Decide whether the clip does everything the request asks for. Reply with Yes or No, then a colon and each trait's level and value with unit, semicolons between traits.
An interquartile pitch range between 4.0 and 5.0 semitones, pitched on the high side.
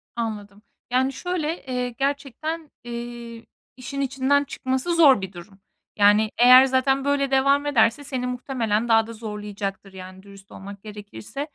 Yes: average, 4.7 semitones; high, 245 Hz